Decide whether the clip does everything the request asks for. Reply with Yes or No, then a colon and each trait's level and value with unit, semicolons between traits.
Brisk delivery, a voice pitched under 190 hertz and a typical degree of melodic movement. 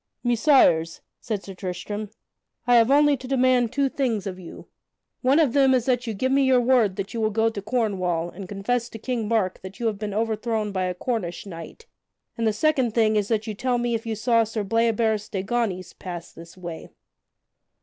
No: fast, 210 wpm; high, 225 Hz; average, 3.9 semitones